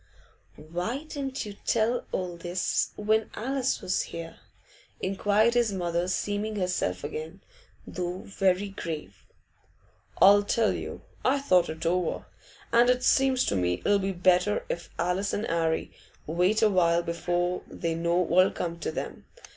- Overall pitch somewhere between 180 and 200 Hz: Yes, medium, 185 Hz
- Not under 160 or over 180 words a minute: No, average, 145 wpm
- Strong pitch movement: No, average, 4.0 semitones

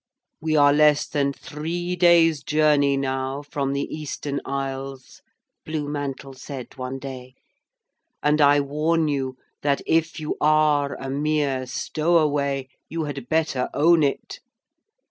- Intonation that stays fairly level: Yes, narrow, 2.0 semitones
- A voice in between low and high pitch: Yes, medium, 145 Hz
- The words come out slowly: Yes, slow, 130 wpm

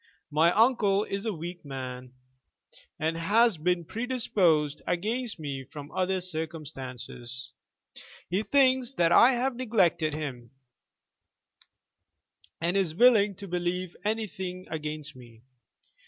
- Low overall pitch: No, medium, 175 Hz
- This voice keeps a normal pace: No, slow, 110 wpm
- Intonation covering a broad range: Yes, wide, 5.7 semitones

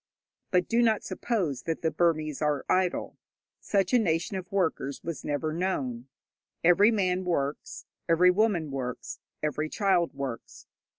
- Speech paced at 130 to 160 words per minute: Yes, average, 140 wpm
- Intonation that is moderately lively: Yes, average, 4.0 semitones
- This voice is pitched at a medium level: Yes, medium, 170 Hz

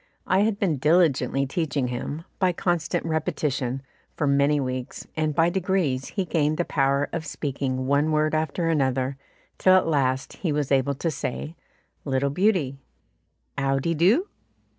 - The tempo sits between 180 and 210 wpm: No, average, 155 wpm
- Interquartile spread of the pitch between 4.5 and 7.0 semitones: No, average, 3.6 semitones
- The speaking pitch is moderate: Yes, medium, 150 Hz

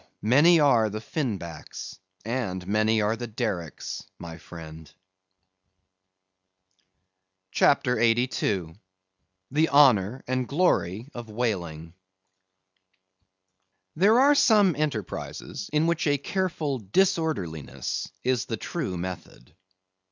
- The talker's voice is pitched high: No, low, 115 Hz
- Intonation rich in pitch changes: Yes, wide, 8.0 semitones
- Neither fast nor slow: No, slow, 100 wpm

